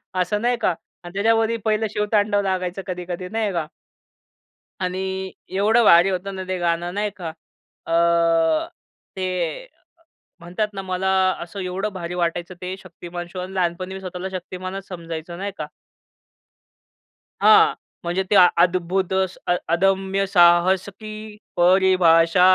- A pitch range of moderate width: No, narrow, 1.9 semitones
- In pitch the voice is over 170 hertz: Yes, medium, 185 Hz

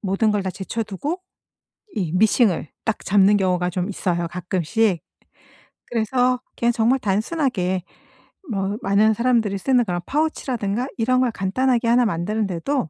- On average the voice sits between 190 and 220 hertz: Yes, high, 210 Hz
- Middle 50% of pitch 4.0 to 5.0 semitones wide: Yes, average, 4.4 semitones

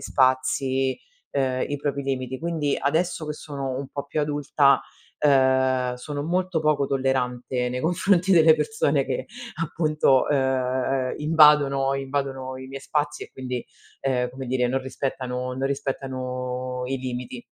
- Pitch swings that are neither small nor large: No, narrow, 2.3 semitones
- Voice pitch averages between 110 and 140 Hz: Yes, low, 135 Hz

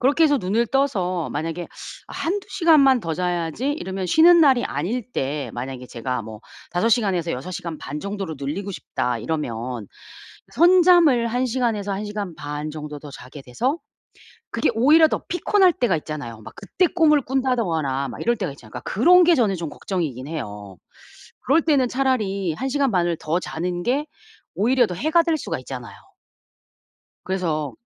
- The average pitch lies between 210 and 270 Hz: No, high, 190 Hz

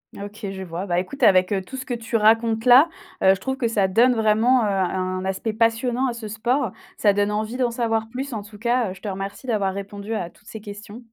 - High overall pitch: Yes, high, 220 Hz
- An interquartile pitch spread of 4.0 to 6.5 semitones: No, average, 3.2 semitones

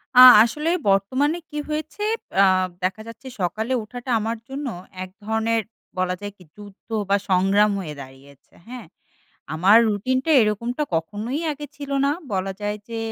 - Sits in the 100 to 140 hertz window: No, high, 215 Hz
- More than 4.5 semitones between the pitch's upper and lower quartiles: Yes, average, 5.0 semitones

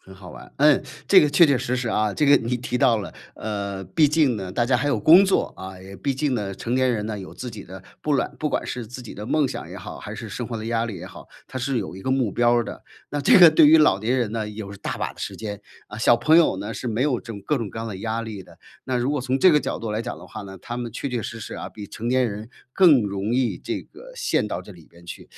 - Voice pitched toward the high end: No, low, 115 Hz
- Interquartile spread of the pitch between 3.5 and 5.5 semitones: Yes, average, 4.3 semitones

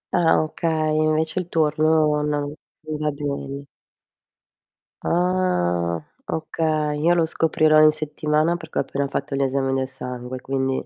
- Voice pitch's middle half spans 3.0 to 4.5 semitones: No, narrow, 2.4 semitones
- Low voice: No, medium, 150 Hz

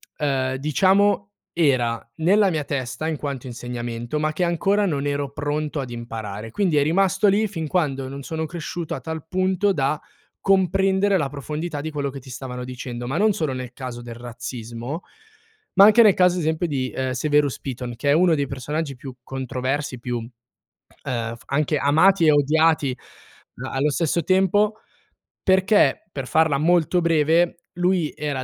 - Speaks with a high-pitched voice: No, medium, 150 Hz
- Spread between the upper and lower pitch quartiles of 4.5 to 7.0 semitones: Yes, average, 5.1 semitones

